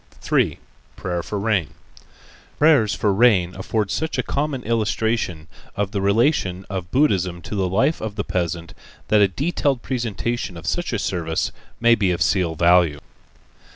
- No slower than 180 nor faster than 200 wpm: No, average, 155 wpm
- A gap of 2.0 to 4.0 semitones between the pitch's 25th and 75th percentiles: No, average, 4.8 semitones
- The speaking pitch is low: Yes, low, 100 Hz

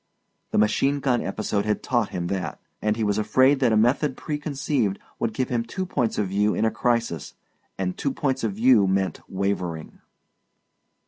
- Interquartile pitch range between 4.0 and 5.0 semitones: Yes, average, 4.7 semitones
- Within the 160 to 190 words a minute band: Yes, average, 180 wpm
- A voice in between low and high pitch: No, low, 110 Hz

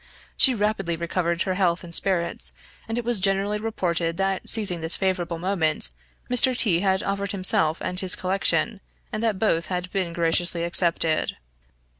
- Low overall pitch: No, medium, 185 Hz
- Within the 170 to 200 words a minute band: No, average, 160 wpm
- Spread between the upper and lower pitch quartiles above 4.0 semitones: No, average, 2.8 semitones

